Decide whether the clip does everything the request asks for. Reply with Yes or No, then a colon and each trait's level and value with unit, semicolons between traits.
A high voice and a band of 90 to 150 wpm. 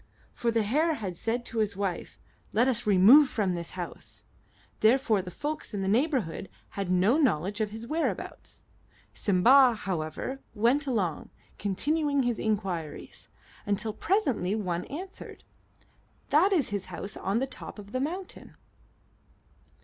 Yes: high, 220 Hz; average, 140 wpm